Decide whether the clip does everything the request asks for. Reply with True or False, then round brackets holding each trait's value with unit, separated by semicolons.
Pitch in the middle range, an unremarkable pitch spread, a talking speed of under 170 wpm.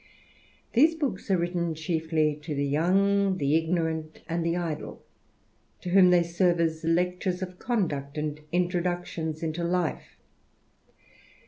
False (170 Hz; 2.2 semitones; 135 wpm)